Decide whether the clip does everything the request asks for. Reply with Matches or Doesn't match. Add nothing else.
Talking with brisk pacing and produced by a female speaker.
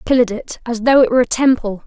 Matches